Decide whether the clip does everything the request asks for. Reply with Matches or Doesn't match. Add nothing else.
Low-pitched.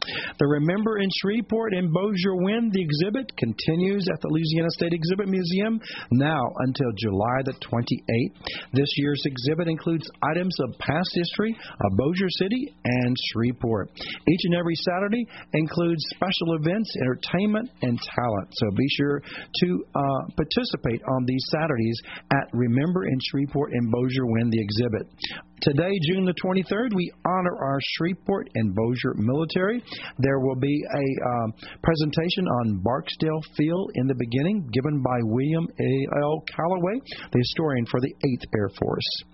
Doesn't match